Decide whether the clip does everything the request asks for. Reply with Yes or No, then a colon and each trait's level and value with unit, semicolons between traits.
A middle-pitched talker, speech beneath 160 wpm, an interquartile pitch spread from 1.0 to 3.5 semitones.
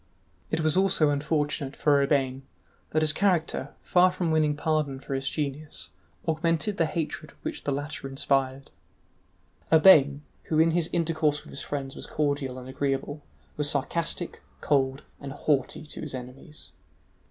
Yes: medium, 150 Hz; average, 150 wpm; narrow, 2.5 semitones